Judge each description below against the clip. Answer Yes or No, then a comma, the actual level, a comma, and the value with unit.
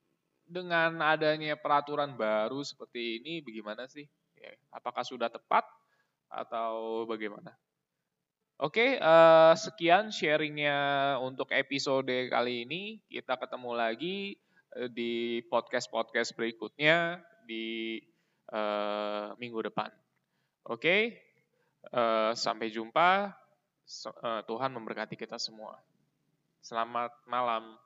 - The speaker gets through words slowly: Yes, slow, 80 wpm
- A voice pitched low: Yes, low, 120 Hz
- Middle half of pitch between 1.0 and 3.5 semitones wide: No, wide, 5.4 semitones